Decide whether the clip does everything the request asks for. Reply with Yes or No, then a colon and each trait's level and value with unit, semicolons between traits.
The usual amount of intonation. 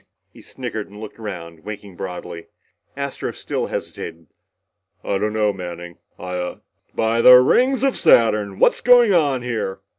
No: wide, 5.7 semitones